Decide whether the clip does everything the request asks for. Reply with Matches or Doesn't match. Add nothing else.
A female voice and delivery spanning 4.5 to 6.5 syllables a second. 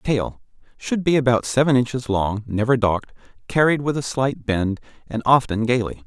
Doesn't match